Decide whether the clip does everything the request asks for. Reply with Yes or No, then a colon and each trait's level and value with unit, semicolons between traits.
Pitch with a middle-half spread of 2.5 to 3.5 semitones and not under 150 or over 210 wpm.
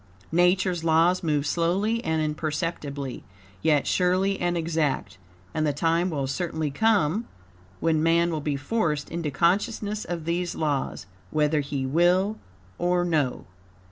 No: average, 3.0 semitones; slow, 135 wpm